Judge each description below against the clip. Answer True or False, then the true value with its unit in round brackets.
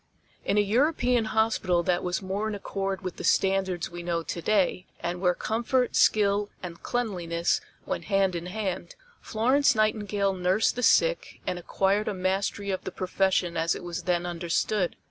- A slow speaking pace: False (170 wpm)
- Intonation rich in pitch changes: False (3.3 semitones)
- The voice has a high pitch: True (195 Hz)